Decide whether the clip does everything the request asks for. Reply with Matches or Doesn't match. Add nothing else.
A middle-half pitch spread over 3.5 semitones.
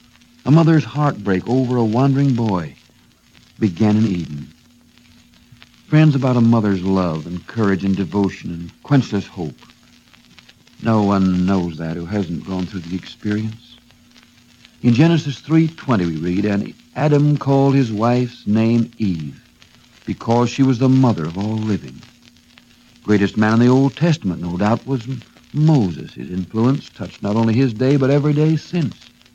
Matches